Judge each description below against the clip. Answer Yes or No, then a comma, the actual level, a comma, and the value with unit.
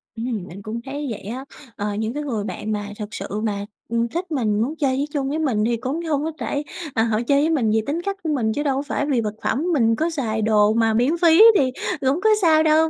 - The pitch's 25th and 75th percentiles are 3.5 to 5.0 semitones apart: No, wide, 5.5 semitones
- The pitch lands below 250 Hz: No, very high, 260 Hz